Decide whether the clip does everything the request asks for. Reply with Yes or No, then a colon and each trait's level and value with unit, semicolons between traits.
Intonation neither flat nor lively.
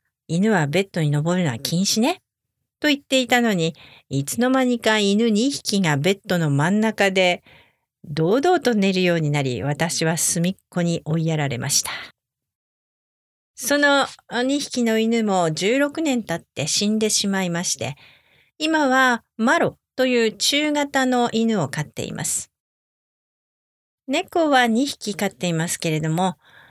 No: wide, 7.1 semitones